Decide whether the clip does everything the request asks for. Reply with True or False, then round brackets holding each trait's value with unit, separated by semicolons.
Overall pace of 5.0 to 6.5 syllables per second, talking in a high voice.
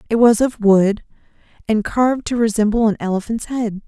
True (5.4 syllables/s; 220 Hz)